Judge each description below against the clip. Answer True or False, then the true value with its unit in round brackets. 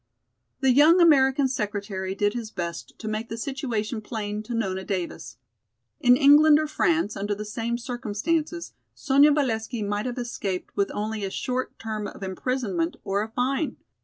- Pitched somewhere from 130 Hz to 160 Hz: False (225 Hz)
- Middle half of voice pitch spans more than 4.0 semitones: True (4.5 semitones)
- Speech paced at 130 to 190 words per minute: True (160 wpm)